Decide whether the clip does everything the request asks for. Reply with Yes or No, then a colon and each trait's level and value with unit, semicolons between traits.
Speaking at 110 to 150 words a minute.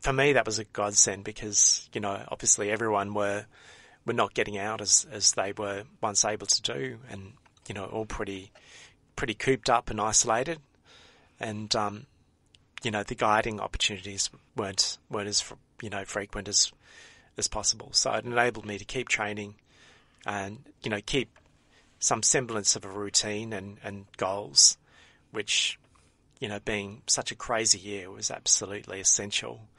No: average, 160 wpm